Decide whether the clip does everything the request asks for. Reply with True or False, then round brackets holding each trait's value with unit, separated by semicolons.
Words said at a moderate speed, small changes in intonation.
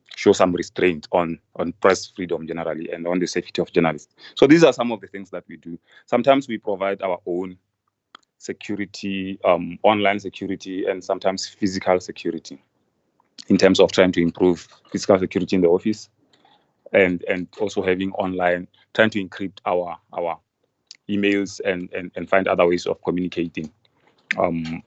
True (165 wpm; 2.2 semitones)